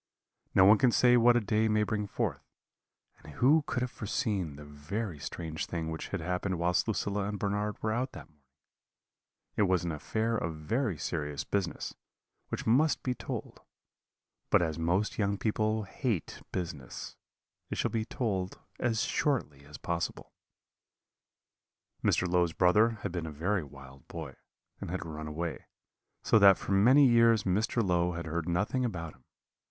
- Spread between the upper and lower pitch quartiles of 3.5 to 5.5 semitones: Yes, average, 5.1 semitones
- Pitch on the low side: Yes, very low, 95 Hz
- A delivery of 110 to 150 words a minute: No, average, 165 wpm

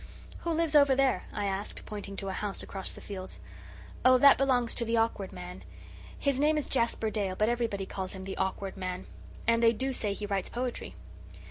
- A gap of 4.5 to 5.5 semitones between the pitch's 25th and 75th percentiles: Yes, average, 4.9 semitones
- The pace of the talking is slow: No, fast, 205 wpm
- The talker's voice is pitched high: Yes, high, 215 Hz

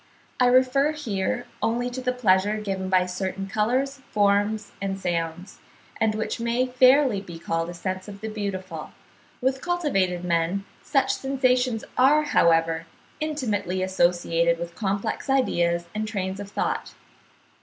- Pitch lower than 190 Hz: No, high, 205 Hz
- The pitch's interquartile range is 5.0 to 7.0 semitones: Yes, wide, 5.4 semitones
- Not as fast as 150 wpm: Yes, average, 140 wpm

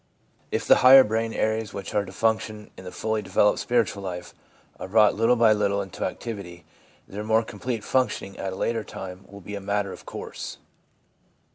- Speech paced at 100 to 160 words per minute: No, average, 185 wpm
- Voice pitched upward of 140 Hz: No, low, 105 Hz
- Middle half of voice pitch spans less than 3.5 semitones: Yes, narrow, 2.4 semitones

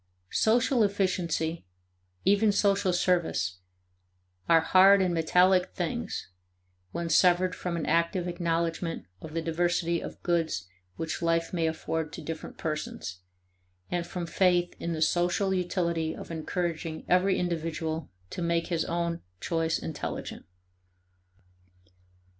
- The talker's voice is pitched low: No, medium, 170 Hz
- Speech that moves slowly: Yes, slow, 120 wpm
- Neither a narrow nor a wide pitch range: No, narrow, 1.8 semitones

